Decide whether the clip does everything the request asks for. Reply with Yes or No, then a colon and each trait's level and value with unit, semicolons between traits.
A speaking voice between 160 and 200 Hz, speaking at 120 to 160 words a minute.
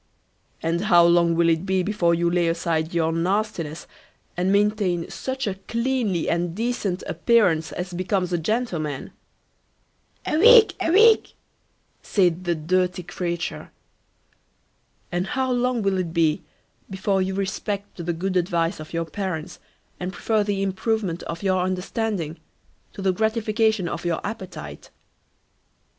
Yes: medium, 185 Hz; average, 140 wpm